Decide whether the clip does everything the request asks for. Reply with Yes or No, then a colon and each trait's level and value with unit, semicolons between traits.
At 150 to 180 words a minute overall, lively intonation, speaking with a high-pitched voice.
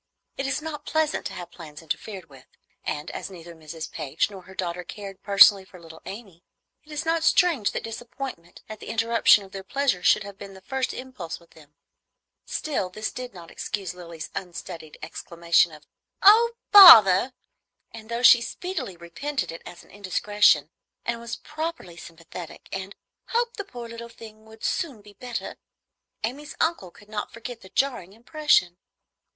Yes: average, 170 wpm; wide, 6.5 semitones; high, 205 Hz